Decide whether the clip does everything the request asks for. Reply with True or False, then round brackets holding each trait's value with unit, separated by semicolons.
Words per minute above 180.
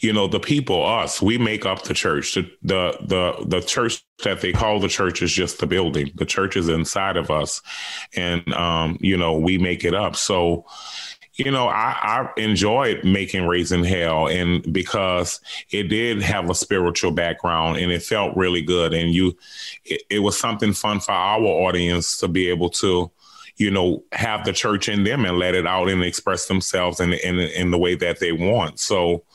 True (200 wpm)